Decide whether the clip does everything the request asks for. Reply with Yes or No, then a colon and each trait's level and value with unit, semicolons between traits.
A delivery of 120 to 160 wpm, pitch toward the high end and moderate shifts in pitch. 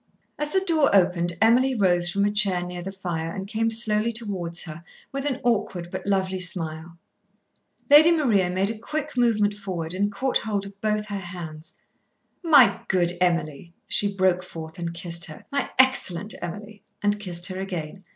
No: average, 175 wpm; high, 195 Hz; average, 4.1 semitones